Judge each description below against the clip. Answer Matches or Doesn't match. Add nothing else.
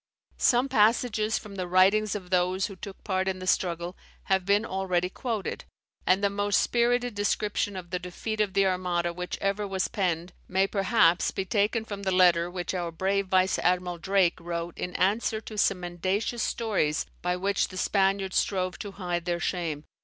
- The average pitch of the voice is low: Doesn't match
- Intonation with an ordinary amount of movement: Doesn't match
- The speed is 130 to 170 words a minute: Doesn't match